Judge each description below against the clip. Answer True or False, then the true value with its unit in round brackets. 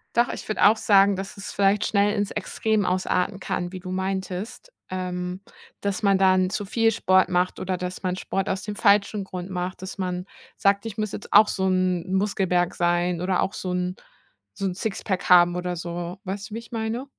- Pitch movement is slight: True (2.0 semitones)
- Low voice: False (190 Hz)